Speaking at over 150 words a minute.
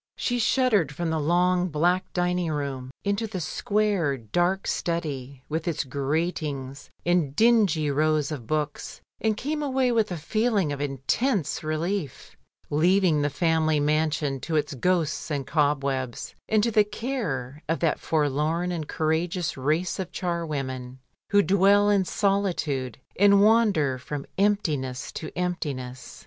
No: average, 140 wpm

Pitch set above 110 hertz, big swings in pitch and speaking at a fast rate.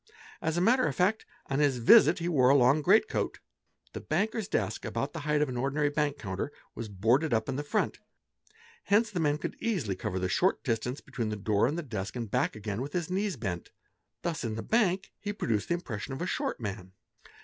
Yes: medium, 140 Hz; wide, 7.5 semitones; fast, 225 wpm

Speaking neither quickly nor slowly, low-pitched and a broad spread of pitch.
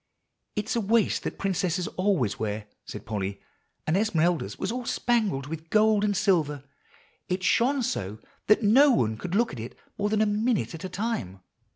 No: average, 180 wpm; high, 190 Hz; wide, 6.7 semitones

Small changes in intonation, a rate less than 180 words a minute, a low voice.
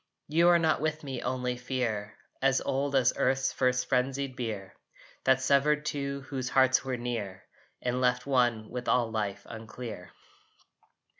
Yes: narrow, 2.1 semitones; average, 150 wpm; low, 130 Hz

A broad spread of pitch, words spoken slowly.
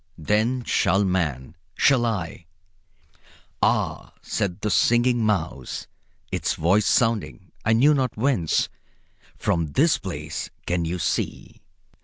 Yes: wide, 6.0 semitones; slow, 120 wpm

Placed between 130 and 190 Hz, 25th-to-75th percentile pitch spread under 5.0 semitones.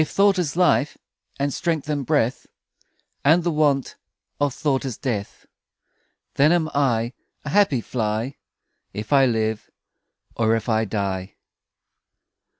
No: low, 135 Hz; average, 5.3 semitones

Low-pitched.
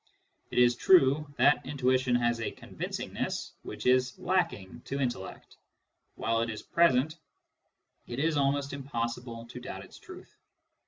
Yes: low, 130 Hz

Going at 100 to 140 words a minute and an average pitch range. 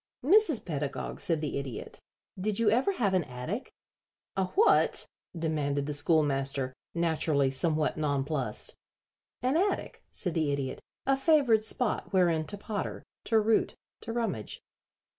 No: slow, 135 wpm; wide, 7.7 semitones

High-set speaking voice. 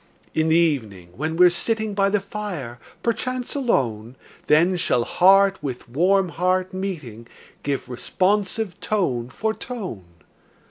No: medium, 180 Hz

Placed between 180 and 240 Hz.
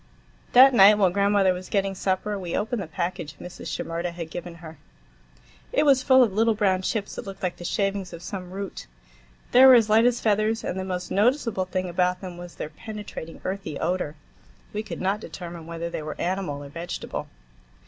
Yes: high, 190 Hz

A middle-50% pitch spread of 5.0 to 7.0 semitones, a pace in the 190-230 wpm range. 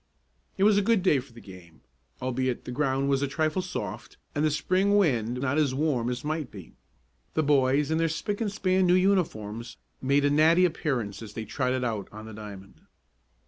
Yes: wide, 5.6 semitones; average, 200 wpm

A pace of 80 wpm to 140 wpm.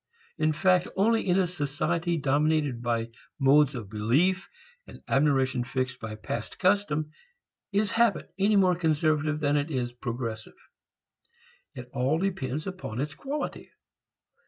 Yes: slow, 135 wpm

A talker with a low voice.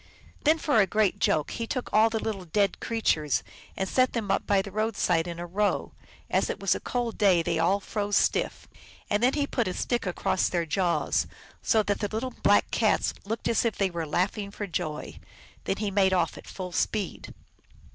No: high, 200 Hz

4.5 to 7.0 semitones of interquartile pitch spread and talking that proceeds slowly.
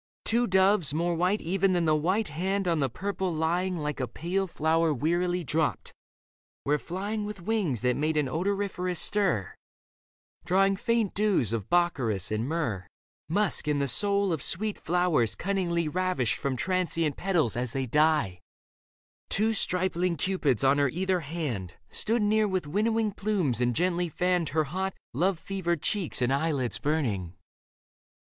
No: average, 4.9 semitones; average, 155 wpm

